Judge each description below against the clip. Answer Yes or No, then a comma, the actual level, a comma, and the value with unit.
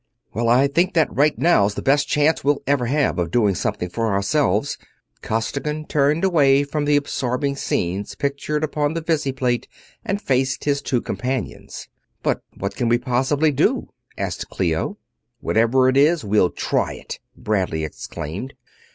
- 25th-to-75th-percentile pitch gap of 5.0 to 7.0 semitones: No, average, 4.6 semitones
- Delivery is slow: No, average, 155 wpm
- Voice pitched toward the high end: No, low, 135 Hz